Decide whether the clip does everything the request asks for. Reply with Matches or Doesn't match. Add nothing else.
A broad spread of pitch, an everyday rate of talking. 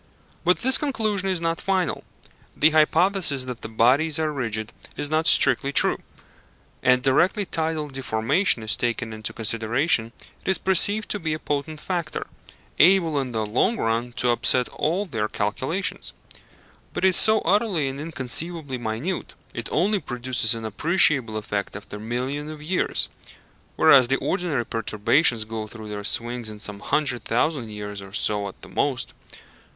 Matches